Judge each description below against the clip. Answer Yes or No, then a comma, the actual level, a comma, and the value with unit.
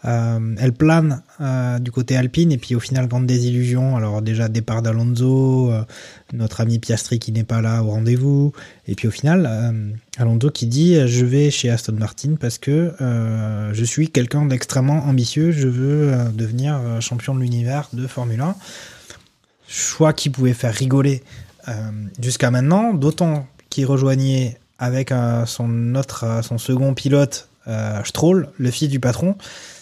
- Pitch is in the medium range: No, low, 125 Hz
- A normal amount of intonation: Yes, average, 3.3 semitones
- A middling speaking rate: Yes, average, 175 wpm